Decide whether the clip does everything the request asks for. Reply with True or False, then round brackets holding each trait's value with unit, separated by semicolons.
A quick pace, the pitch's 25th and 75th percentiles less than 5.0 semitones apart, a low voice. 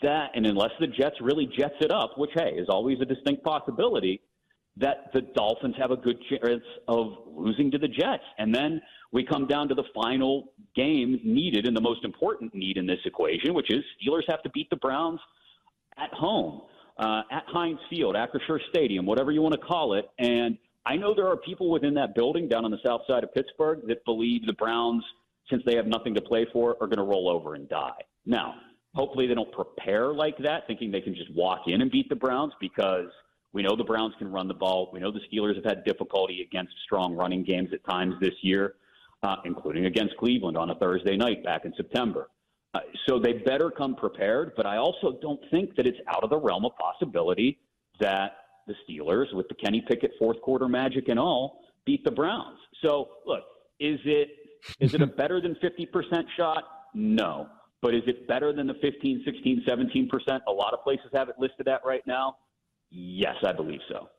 False (210 wpm; 5.4 semitones; 130 Hz)